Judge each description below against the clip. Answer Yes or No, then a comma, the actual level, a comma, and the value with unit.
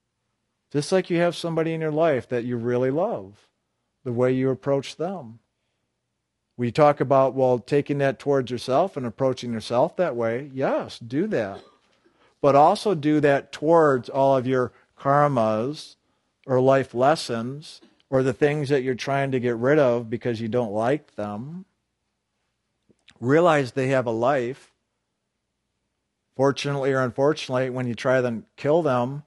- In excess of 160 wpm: No, average, 150 wpm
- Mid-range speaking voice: No, low, 130 Hz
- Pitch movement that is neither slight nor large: Yes, average, 3.1 semitones